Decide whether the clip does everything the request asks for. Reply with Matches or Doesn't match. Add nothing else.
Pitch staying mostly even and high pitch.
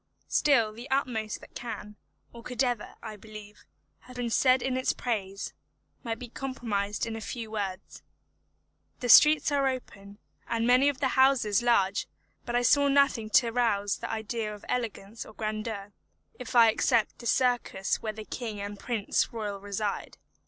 Doesn't match